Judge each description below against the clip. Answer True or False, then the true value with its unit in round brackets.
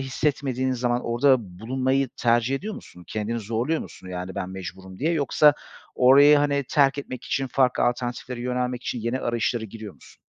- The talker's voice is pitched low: True (125 Hz)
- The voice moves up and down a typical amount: True (3.0 semitones)